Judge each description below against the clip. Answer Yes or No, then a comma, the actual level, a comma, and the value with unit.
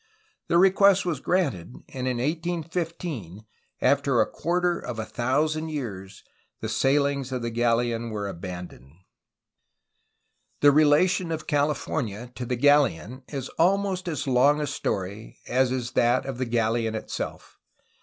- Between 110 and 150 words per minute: Yes, slow, 135 wpm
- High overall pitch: No, low, 130 Hz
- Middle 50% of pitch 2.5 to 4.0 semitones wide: No, average, 5.3 semitones